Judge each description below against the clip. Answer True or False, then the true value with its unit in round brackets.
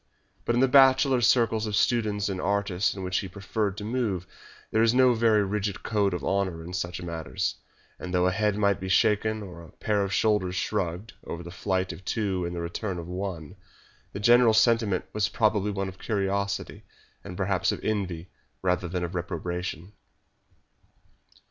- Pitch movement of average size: True (3.1 semitones)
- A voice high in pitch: False (100 Hz)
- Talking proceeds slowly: False (180 wpm)